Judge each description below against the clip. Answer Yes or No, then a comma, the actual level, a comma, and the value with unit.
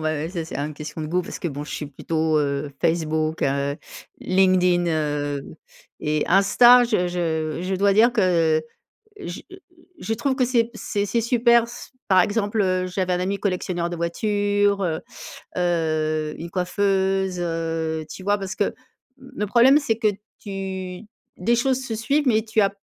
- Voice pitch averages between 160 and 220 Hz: Yes, medium, 185 Hz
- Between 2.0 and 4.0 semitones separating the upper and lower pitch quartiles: No, average, 4.7 semitones